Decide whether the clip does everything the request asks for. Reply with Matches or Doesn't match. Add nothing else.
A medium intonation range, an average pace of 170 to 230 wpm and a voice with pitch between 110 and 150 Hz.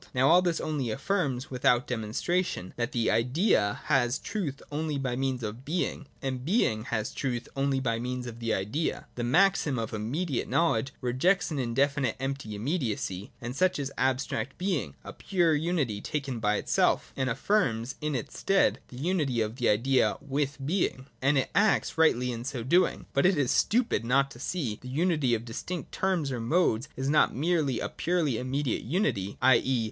Matches